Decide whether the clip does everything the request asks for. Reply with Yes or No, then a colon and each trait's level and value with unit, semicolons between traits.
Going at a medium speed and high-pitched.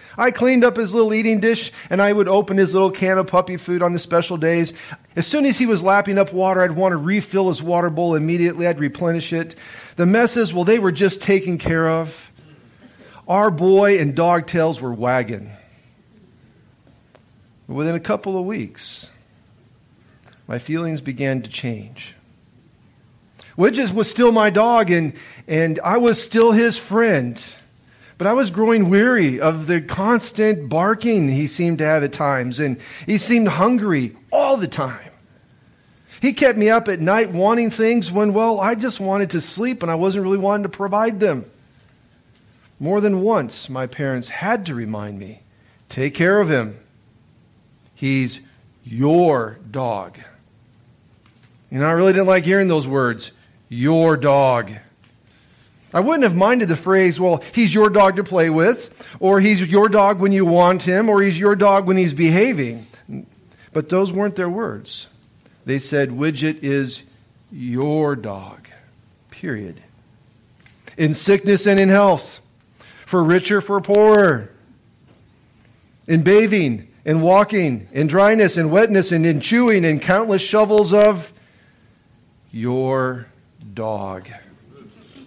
No: average, 150 wpm; medium, 175 Hz